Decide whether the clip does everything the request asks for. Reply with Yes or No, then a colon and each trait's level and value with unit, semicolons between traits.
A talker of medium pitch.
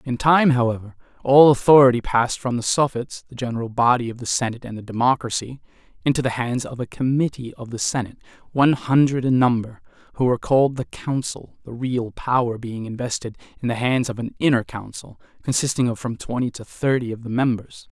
No: low, 125 Hz